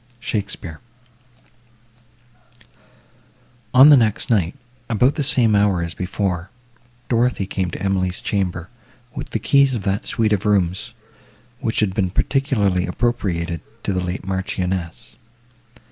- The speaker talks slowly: Yes, slow, 125 wpm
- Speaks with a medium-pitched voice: No, low, 100 Hz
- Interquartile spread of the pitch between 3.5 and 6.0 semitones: Yes, average, 3.9 semitones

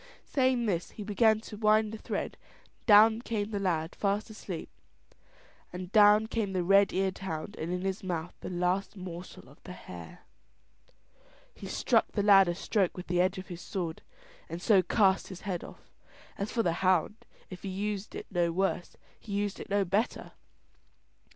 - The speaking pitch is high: Yes, high, 195 Hz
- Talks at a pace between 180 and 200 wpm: Yes, average, 185 wpm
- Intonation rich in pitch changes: No, average, 2.8 semitones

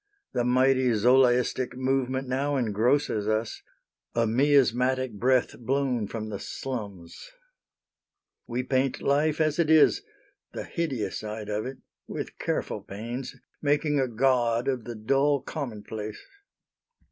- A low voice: Yes, low, 125 Hz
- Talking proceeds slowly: Yes, slow, 125 wpm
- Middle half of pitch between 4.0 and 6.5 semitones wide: No, average, 3.2 semitones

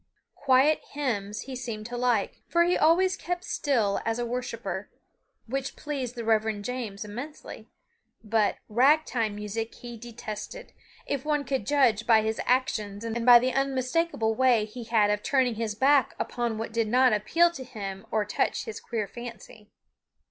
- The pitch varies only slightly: No, average, 3.6 semitones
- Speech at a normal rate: Yes, average, 165 wpm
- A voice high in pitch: Yes, high, 235 Hz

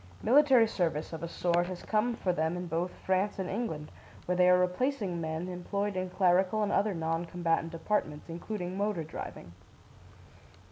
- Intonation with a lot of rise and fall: No, average, 3.5 semitones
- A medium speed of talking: Yes, average, 170 wpm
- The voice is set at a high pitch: No, medium, 180 Hz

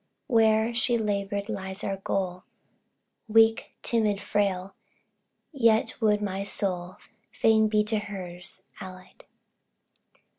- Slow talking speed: Yes, slow, 105 wpm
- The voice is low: No, high, 205 Hz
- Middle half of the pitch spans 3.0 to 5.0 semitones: No, narrow, 2.5 semitones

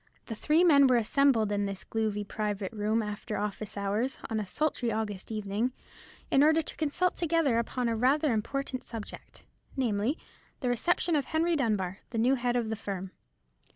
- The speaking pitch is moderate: No, high, 230 Hz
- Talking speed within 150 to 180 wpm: Yes, average, 175 wpm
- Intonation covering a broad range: No, average, 4.8 semitones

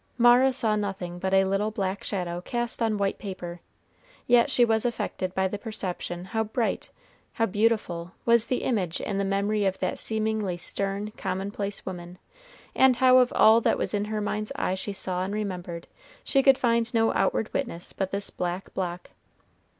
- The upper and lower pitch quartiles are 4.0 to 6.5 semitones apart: No, average, 3.3 semitones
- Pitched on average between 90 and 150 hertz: No, high, 205 Hz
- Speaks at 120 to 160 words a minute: No, average, 175 wpm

